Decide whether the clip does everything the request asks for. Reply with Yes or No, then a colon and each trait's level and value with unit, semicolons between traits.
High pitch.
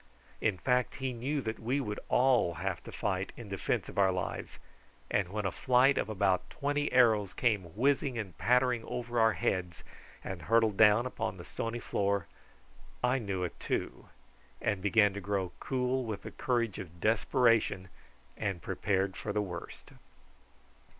No: low, 110 Hz